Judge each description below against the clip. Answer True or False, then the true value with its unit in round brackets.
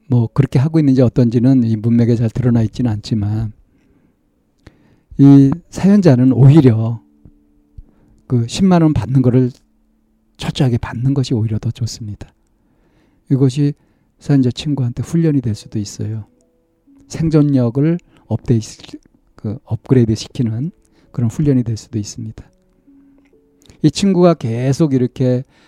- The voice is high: False (125 Hz)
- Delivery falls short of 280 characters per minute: True (265 characters per minute)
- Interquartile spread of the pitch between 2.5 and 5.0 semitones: True (4.6 semitones)